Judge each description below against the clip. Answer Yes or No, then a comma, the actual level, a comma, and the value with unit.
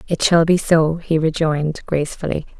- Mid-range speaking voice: Yes, medium, 160 Hz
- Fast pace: No, average, 160 wpm